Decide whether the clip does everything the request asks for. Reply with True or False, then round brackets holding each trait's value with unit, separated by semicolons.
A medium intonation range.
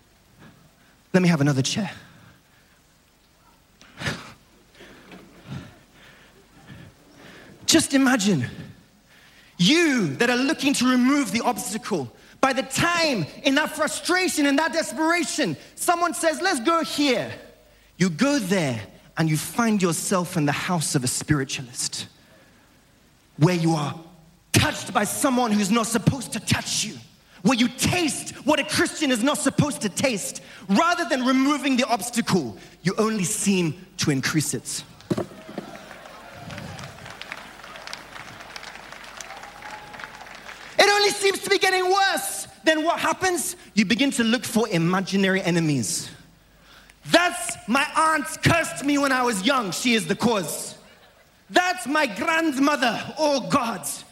False (9.0 semitones)